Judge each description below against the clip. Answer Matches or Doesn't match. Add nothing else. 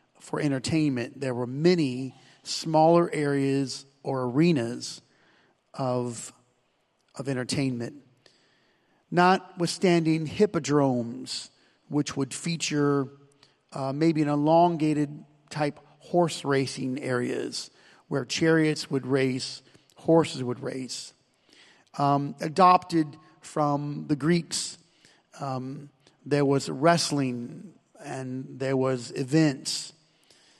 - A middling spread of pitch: Matches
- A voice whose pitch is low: Doesn't match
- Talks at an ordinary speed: Doesn't match